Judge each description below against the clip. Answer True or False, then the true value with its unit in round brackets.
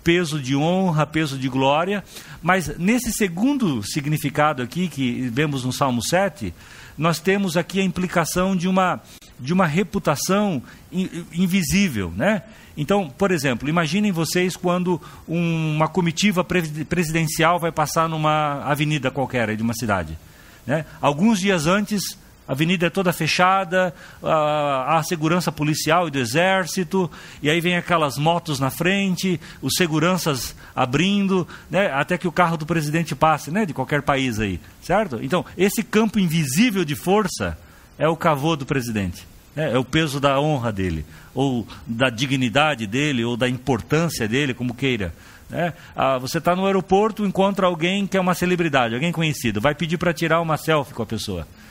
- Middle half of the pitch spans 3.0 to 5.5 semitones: True (5.1 semitones)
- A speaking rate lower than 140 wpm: False (155 wpm)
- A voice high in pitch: False (160 Hz)